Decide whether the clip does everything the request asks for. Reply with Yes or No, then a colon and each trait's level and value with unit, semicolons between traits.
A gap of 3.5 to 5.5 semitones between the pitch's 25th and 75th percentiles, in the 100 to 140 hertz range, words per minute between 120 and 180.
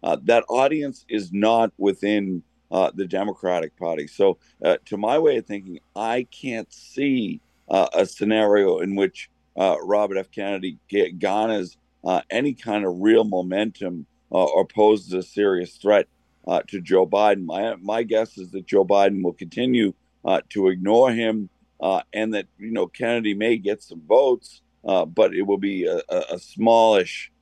No: narrow, 2.6 semitones; low, 105 Hz; average, 170 wpm